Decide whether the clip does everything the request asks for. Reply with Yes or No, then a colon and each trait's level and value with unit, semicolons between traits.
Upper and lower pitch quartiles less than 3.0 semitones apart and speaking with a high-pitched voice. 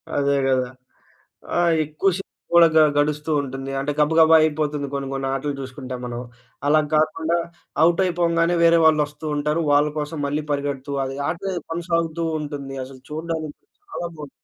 No: narrow, 2.6 semitones; medium, 150 Hz